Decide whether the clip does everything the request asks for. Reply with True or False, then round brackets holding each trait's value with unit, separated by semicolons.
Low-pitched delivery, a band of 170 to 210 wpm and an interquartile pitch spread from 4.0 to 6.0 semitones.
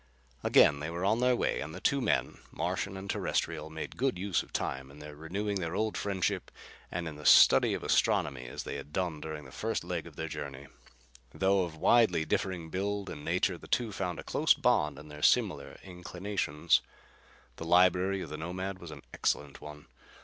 True (85 Hz; 200 wpm; 4.3 semitones)